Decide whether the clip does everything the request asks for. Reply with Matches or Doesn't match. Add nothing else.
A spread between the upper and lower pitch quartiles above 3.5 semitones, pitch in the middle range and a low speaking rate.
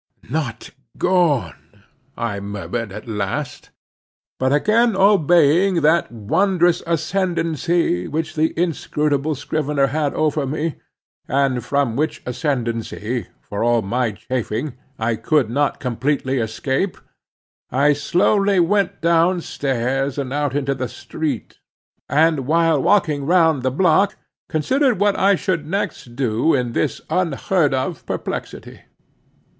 Matches